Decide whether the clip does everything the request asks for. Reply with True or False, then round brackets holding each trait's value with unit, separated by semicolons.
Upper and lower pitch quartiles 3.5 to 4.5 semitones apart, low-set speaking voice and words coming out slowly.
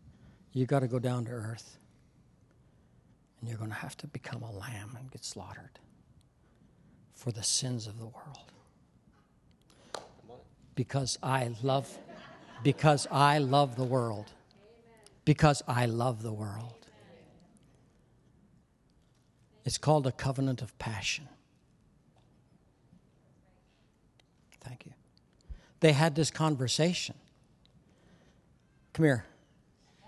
True (3.8 semitones; 130 Hz; 105 wpm)